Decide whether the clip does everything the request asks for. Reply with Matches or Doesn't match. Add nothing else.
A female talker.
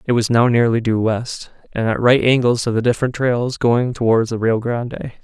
Doesn't match